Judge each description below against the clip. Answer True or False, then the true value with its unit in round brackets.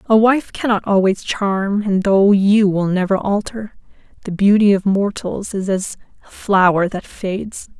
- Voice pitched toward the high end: True (200 Hz)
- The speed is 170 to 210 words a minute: False (160 wpm)